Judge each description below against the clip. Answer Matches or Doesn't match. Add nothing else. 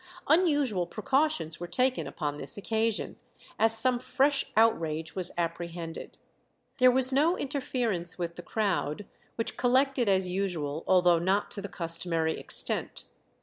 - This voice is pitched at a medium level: Doesn't match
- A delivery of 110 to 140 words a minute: Matches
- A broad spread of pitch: Matches